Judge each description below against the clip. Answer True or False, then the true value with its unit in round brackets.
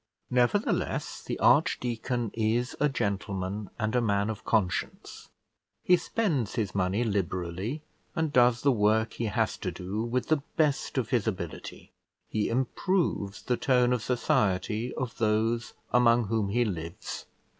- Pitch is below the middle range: True (115 Hz)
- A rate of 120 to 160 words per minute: True (145 wpm)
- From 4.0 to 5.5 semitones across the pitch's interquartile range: False (3.5 semitones)